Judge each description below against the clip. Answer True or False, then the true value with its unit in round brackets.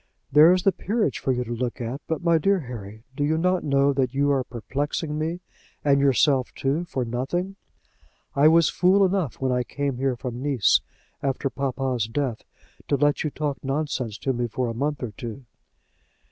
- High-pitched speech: False (140 Hz)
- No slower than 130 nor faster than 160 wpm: False (190 wpm)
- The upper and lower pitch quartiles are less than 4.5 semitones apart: True (3.6 semitones)